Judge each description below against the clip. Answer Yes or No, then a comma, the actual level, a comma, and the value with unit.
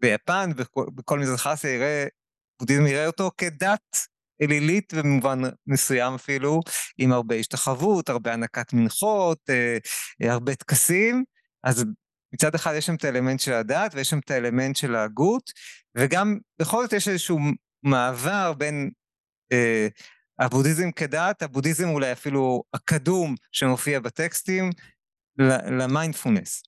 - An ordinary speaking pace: Yes, average, 120 wpm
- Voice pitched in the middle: Yes, medium, 145 Hz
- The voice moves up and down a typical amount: Yes, average, 5.0 semitones